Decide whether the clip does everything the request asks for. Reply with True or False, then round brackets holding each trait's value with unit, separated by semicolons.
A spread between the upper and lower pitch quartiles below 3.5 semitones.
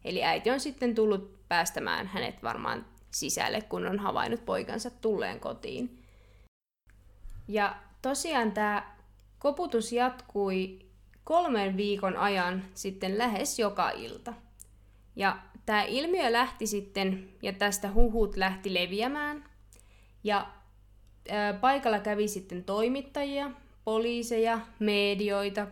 False (4.0 semitones)